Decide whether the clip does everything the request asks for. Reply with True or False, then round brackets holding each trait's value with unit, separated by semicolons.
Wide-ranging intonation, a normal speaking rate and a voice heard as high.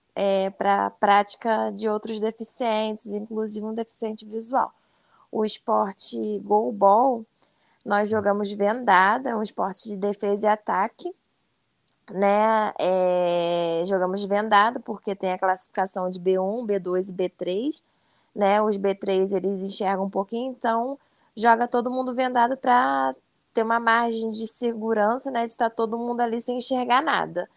False (3.0 semitones; 140 wpm; 215 Hz)